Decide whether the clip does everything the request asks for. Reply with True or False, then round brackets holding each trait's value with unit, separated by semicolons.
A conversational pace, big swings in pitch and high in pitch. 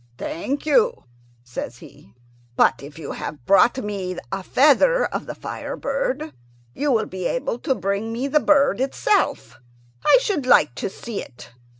True (165 wpm; 8.1 semitones; 235 Hz)